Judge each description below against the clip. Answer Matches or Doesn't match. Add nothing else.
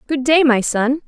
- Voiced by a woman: Matches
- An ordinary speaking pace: Doesn't match